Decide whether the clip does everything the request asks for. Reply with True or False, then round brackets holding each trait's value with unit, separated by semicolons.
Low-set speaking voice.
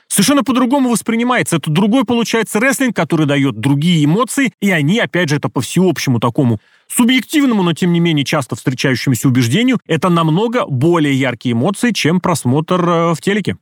False (170 Hz)